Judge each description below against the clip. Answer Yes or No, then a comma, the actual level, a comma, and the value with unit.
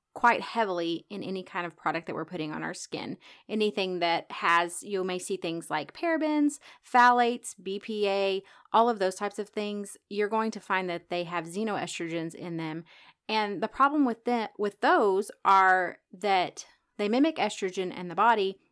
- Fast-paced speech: No, average, 175 wpm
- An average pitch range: Yes, average, 3.8 semitones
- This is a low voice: No, high, 200 Hz